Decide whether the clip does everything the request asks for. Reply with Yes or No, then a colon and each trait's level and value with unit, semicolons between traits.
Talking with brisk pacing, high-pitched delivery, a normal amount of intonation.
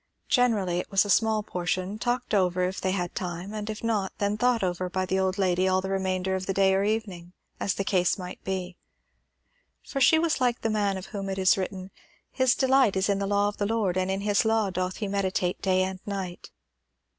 No: fast, 225 wpm; high, 195 Hz; narrow, 2.3 semitones